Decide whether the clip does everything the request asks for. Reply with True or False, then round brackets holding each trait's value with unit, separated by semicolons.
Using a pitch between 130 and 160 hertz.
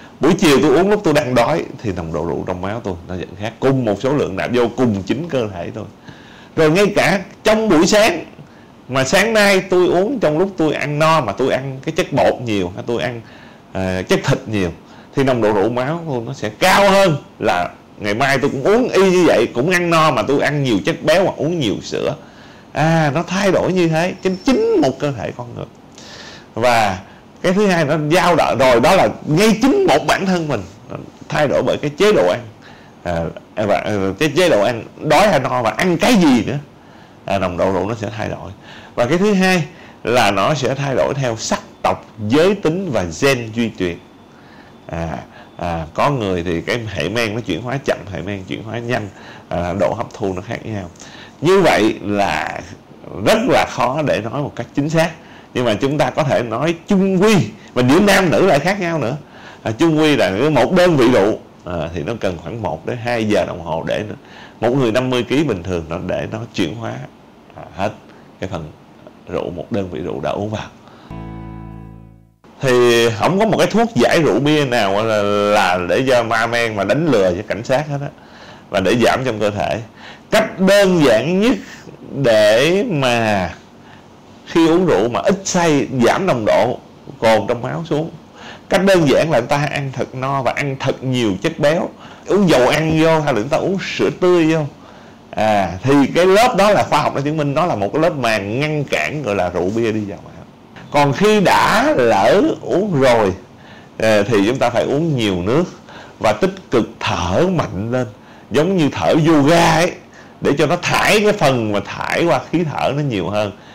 True (140 Hz)